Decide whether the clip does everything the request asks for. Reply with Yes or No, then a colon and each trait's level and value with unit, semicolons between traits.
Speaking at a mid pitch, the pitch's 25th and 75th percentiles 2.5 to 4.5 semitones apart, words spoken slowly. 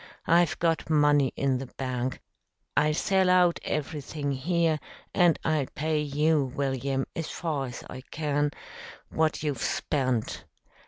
Yes: medium, 150 Hz; average, 3.0 semitones; slow, 130 wpm